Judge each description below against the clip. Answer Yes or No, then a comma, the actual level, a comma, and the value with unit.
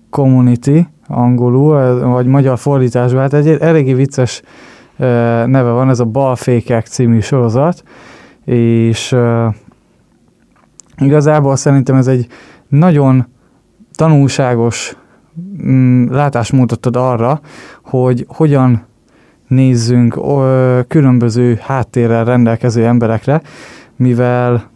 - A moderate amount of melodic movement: No, narrow, 2.3 semitones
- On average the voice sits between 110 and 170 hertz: Yes, low, 125 Hz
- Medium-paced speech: No, slow, 80 wpm